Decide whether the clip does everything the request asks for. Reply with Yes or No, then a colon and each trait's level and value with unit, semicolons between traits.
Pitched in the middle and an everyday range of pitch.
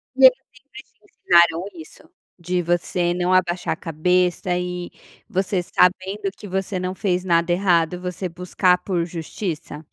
No: medium, 180 Hz; narrow, 1.4 semitones